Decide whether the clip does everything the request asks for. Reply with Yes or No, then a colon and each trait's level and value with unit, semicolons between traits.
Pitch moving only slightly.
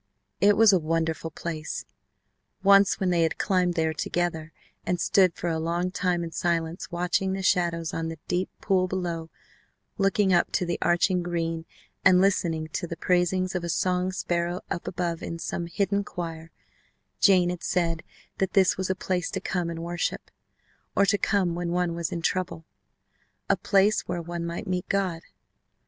Yes: narrow, 1.9 semitones